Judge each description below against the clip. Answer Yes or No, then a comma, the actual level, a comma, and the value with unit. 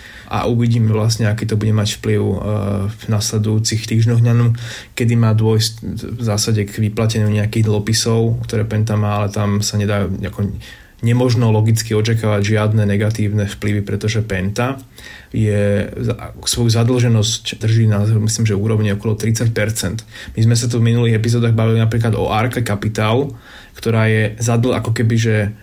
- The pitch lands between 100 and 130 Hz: Yes, low, 110 Hz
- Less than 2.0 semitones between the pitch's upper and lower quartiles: Yes, narrow, 1.6 semitones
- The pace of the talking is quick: No, average, 150 wpm